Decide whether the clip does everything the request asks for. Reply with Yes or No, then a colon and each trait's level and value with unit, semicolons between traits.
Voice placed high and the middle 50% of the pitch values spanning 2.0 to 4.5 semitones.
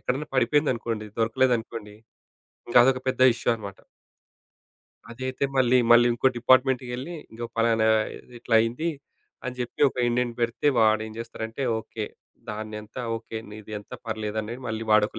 No: low, 115 Hz; narrow, 2.4 semitones